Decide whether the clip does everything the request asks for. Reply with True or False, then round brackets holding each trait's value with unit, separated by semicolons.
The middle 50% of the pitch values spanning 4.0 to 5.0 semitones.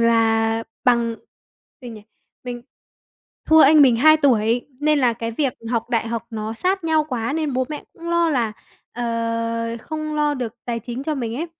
True (4.7 semitones)